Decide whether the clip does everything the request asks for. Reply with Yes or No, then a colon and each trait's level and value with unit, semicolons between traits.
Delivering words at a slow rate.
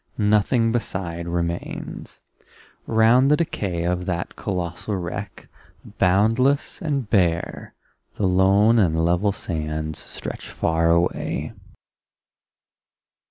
Yes: slow, 95 wpm